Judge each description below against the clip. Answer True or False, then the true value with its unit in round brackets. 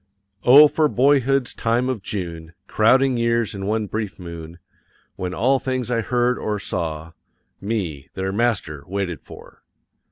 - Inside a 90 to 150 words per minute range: True (140 wpm)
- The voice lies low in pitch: True (110 Hz)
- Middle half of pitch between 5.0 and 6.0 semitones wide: True (5.5 semitones)